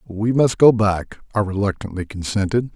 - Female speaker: No, male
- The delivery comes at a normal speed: Yes, average, 150 wpm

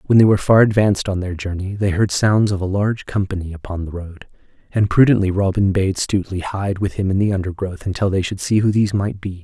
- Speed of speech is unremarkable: No, fast, 235 wpm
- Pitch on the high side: No, very low, 95 Hz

